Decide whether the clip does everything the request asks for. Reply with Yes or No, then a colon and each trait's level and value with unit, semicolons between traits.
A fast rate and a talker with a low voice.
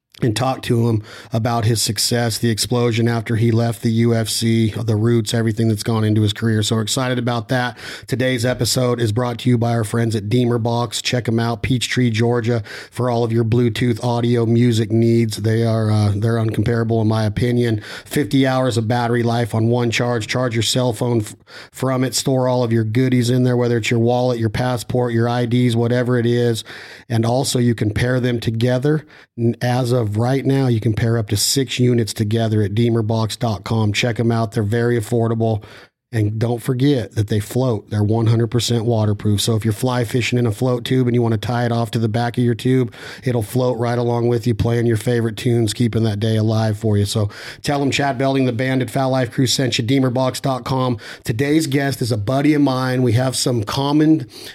Yes: fast, 210 wpm; low, 120 Hz